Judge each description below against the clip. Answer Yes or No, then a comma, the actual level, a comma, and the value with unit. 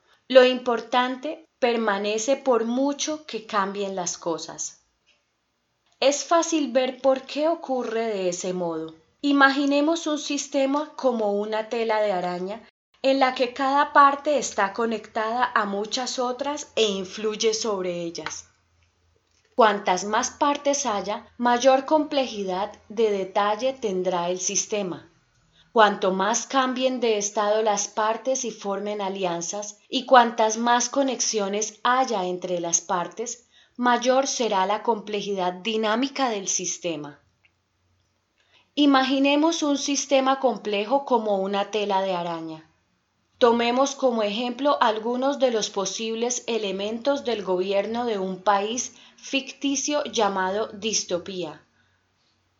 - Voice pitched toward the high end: Yes, high, 225 Hz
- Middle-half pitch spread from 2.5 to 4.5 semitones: No, average, 5.0 semitones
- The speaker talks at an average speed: No, slow, 115 wpm